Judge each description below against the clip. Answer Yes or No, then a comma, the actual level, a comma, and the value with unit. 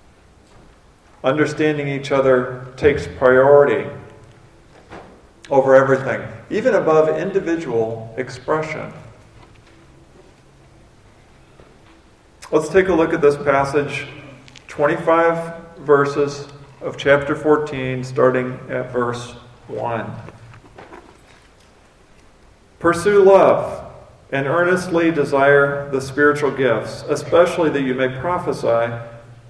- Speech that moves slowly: Yes, slow, 80 wpm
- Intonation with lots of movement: No, average, 3.8 semitones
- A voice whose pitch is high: No, medium, 140 Hz